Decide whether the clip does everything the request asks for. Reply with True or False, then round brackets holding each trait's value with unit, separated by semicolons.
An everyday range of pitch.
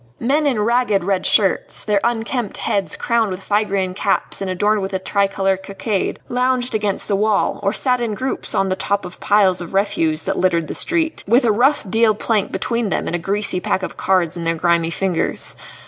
True (3.4 semitones)